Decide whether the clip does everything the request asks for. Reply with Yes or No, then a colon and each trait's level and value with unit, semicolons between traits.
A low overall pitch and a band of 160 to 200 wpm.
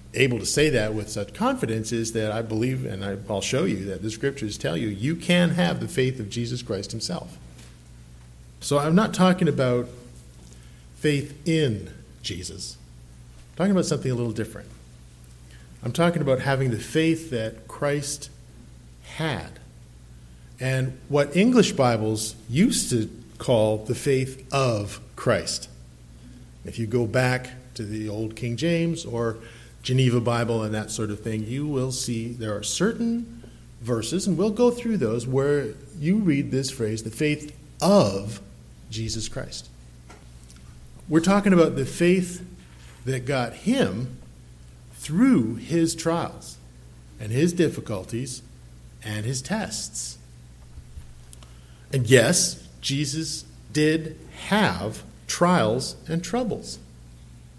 No: low, 115 Hz; slow, 135 wpm